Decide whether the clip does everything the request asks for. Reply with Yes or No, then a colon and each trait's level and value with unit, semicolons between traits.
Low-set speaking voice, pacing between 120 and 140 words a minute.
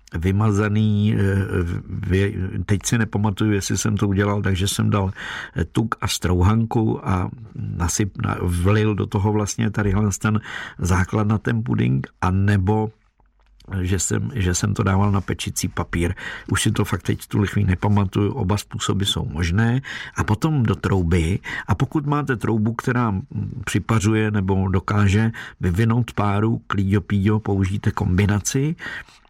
Yes: low, 105 Hz; average, 135 wpm